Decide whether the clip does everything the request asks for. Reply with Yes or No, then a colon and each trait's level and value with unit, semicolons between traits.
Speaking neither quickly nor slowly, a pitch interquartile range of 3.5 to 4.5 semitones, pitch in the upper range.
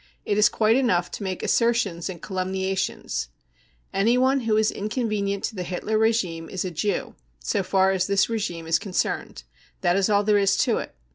No: average, 185 wpm; average, 3.0 semitones; high, 195 Hz